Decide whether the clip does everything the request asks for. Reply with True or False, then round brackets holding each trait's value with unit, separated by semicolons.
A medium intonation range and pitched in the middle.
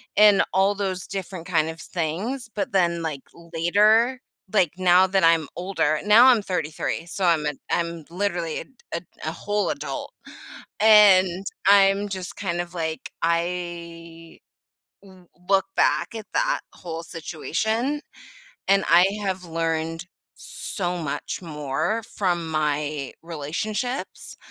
True (3.4 semitones; 175 Hz)